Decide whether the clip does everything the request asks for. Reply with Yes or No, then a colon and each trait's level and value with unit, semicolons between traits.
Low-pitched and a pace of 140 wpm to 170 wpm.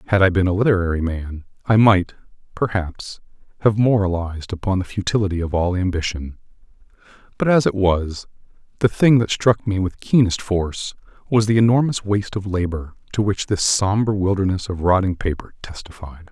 Yes: very low, 95 Hz; average, 160 wpm